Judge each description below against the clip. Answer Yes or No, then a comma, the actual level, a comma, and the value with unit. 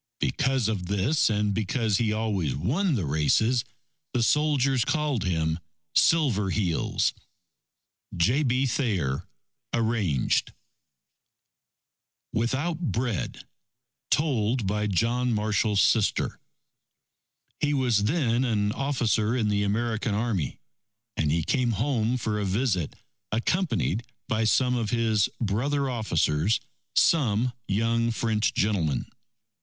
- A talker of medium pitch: No, low, 110 Hz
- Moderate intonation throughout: Yes, average, 3.7 semitones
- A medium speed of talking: No, slow, 110 wpm